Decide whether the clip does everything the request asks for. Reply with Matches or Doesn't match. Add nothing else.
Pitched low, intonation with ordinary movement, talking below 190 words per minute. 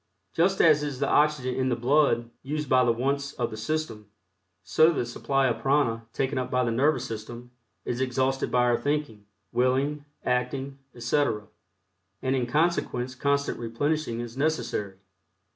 Matches